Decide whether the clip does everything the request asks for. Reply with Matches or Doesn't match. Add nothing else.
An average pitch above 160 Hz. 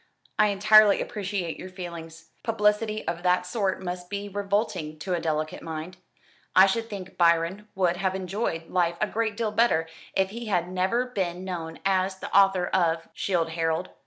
Matches